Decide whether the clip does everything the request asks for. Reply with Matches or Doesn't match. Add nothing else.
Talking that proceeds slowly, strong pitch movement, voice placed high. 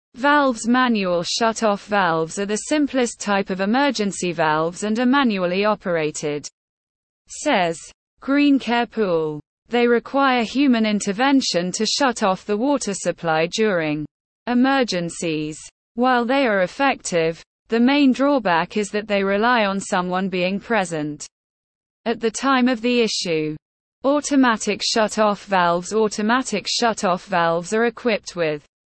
Matches